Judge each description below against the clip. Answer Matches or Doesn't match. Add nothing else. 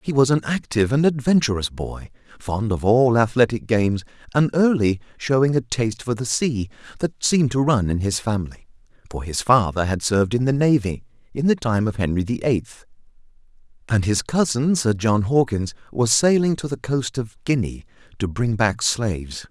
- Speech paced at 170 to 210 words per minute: Matches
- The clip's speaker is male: Matches